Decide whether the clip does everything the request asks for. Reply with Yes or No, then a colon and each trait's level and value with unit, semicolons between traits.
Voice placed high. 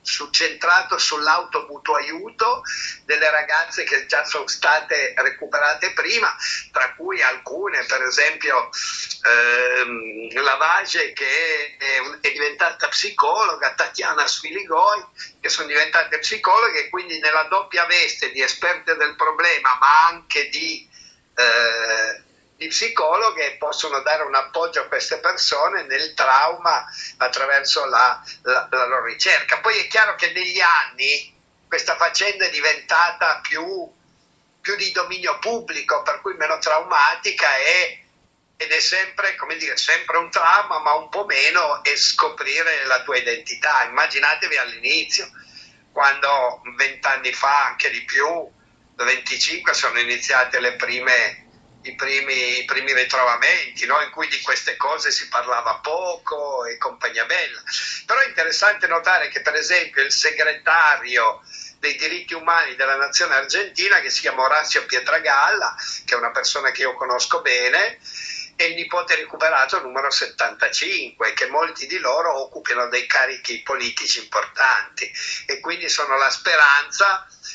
No: medium, 180 Hz